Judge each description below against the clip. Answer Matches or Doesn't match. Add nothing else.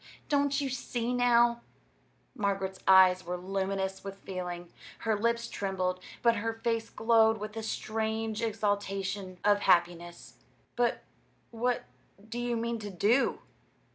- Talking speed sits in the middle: Doesn't match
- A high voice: Matches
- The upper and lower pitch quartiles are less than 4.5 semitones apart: Matches